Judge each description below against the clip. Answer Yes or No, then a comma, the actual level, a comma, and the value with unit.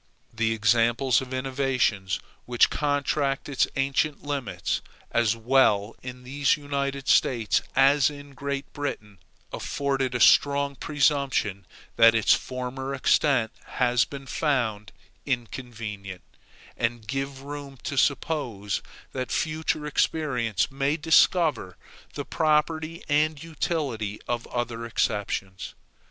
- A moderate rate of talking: No, slow, 110 wpm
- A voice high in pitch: No, low, 130 Hz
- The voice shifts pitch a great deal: No, average, 3.7 semitones